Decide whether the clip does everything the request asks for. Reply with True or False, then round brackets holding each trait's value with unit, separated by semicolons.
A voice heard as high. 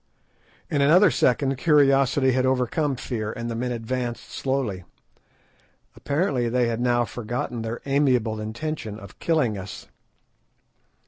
False (125 Hz)